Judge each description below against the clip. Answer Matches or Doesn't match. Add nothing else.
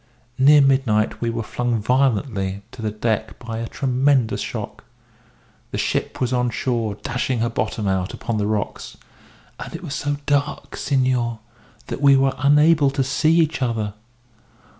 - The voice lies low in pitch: Matches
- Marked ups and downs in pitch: Doesn't match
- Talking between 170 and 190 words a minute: Doesn't match